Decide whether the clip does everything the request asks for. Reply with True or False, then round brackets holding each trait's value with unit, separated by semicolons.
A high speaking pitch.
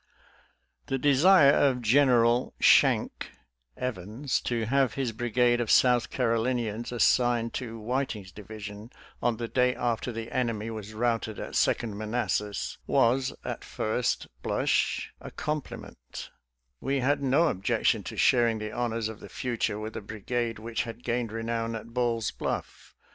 False (115 Hz)